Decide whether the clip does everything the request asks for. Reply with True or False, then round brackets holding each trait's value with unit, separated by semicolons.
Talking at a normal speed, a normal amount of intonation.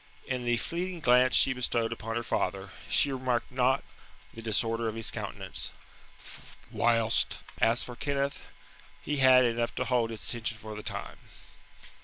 False (155 wpm; 2.3 semitones)